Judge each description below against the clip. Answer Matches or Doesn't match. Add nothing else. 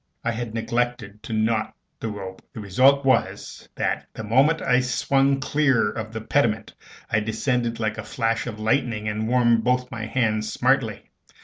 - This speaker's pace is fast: Doesn't match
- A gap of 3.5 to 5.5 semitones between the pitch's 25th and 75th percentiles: Doesn't match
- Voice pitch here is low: Matches